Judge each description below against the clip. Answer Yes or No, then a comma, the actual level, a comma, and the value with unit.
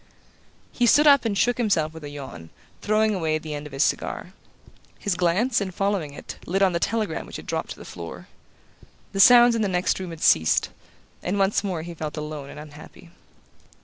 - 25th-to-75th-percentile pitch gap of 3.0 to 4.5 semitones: No, average, 5.2 semitones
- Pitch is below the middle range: No, medium, 180 Hz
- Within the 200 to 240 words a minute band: Yes, fast, 205 wpm